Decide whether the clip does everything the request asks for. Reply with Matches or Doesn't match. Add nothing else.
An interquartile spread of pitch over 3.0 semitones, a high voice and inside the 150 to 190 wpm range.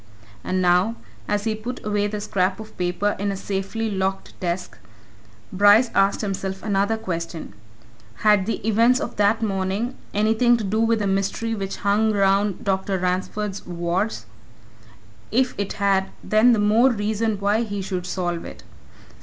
Doesn't match